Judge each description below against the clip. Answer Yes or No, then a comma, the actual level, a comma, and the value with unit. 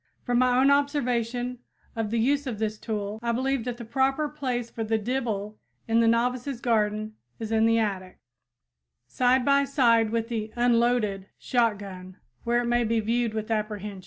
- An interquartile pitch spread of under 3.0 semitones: Yes, narrow, 2.4 semitones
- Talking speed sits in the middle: Yes, average, 175 wpm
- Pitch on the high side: Yes, high, 230 Hz